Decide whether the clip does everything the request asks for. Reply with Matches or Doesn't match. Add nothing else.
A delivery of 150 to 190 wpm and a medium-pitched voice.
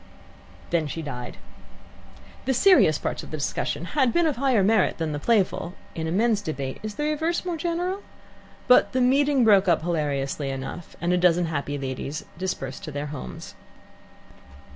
Matches